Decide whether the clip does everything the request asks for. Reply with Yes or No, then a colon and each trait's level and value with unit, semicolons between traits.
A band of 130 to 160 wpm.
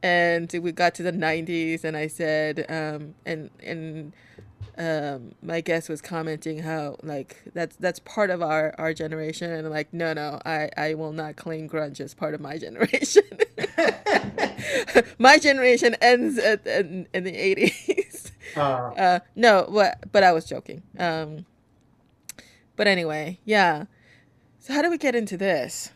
Yes: average, 155 wpm